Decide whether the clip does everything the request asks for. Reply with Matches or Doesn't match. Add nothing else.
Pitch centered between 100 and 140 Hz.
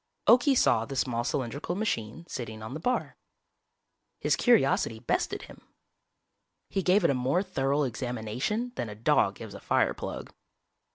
Matches